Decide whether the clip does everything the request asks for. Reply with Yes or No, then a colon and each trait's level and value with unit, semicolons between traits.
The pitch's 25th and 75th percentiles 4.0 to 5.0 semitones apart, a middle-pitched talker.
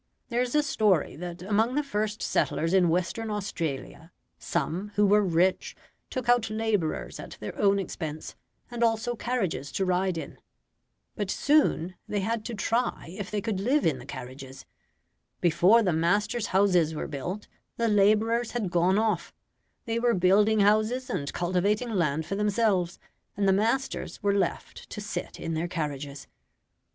No: average, 4.5 semitones; high, 200 Hz